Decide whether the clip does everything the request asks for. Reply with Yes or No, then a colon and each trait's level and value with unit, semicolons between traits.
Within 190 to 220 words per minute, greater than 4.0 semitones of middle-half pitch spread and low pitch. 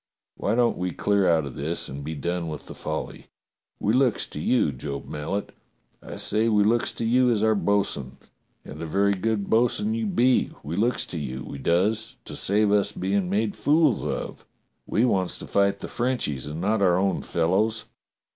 Yes: average, 195 wpm; wide, 5.4 semitones; low, 100 Hz